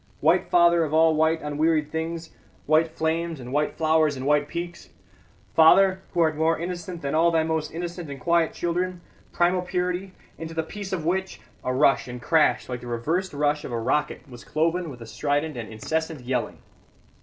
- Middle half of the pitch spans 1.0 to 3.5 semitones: Yes, average, 2.7 semitones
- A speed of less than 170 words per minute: No, average, 190 wpm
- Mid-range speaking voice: Yes, medium, 160 Hz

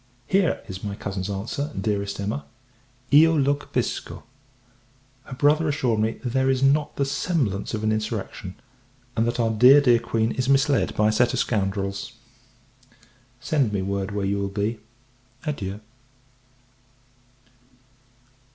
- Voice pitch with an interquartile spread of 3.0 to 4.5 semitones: No, wide, 5.4 semitones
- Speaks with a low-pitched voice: Yes, low, 115 Hz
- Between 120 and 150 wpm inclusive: Yes, average, 140 wpm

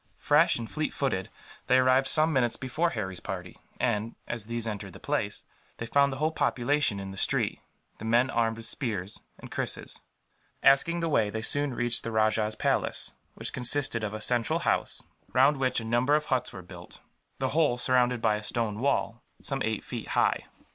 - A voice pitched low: Yes, low, 120 Hz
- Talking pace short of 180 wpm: No, average, 190 wpm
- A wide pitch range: No, average, 3.8 semitones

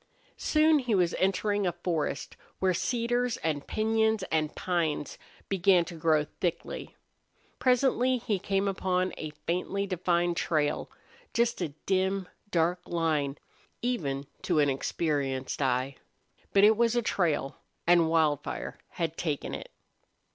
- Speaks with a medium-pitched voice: Yes, medium, 175 Hz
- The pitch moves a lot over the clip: No, average, 4.7 semitones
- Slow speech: Yes, slow, 130 wpm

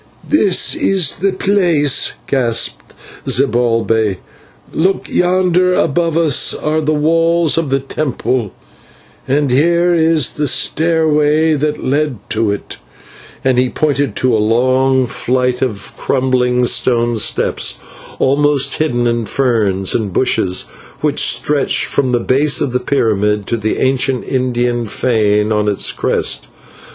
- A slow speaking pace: Yes, slow, 125 wpm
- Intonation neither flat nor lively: Yes, average, 4.5 semitones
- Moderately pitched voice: No, low, 130 Hz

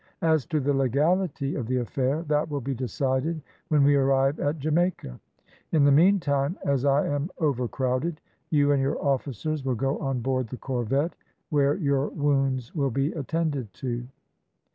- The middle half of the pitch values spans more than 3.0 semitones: No, narrow, 2.4 semitones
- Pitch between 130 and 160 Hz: Yes, medium, 140 Hz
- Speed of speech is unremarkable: Yes, average, 165 wpm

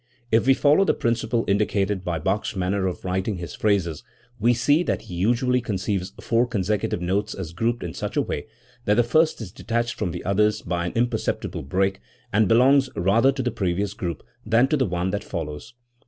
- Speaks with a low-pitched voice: Yes, low, 105 Hz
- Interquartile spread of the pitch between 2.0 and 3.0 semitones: No, average, 4.4 semitones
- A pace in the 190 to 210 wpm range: Yes, average, 200 wpm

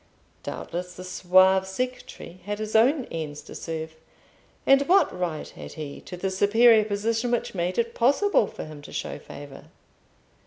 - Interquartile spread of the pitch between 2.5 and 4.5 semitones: No, average, 5.1 semitones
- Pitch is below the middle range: No, high, 190 Hz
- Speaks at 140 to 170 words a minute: Yes, average, 160 wpm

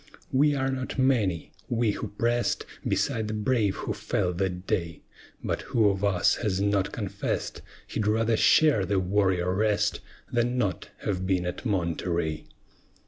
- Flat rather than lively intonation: No, average, 4.0 semitones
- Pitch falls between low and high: No, low, 100 Hz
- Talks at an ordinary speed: Yes, average, 150 wpm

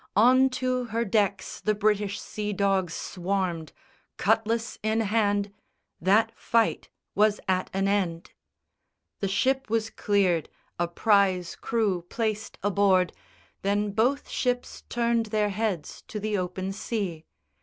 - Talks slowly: Yes, slow, 130 wpm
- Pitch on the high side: Yes, high, 205 Hz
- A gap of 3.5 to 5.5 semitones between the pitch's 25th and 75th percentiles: No, average, 2.8 semitones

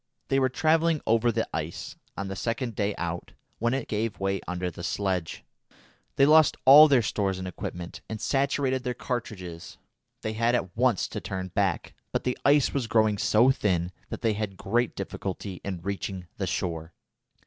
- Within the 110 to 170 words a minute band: No, average, 180 wpm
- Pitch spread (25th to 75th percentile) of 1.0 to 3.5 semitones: No, average, 5.1 semitones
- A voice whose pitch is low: Yes, low, 105 Hz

